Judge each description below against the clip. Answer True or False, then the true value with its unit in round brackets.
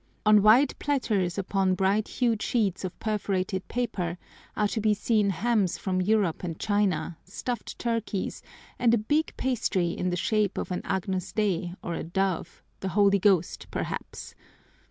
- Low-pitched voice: False (200 Hz)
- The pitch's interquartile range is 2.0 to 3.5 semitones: True (2.9 semitones)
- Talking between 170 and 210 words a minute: False (155 wpm)